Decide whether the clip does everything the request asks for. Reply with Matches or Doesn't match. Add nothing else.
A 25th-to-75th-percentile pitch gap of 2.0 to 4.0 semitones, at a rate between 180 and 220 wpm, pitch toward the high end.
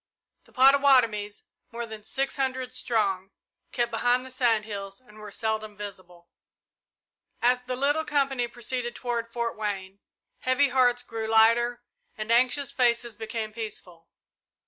Doesn't match